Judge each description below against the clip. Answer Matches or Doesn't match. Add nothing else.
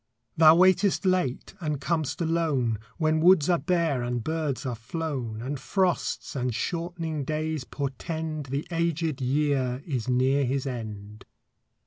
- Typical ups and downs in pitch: Matches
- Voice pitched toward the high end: Doesn't match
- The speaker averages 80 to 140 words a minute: Matches